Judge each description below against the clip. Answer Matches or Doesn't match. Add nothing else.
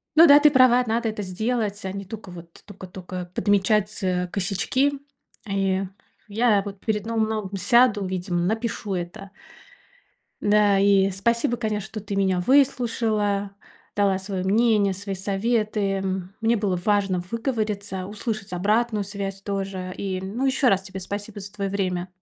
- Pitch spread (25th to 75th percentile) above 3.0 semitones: Doesn't match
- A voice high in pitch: Matches